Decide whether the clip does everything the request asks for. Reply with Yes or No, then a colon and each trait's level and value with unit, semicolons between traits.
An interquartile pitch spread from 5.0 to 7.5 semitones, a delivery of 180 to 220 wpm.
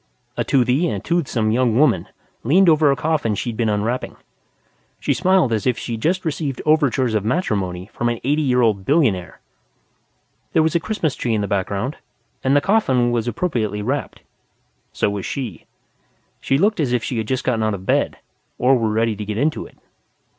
Yes: wide, 5.6 semitones; average, 190 wpm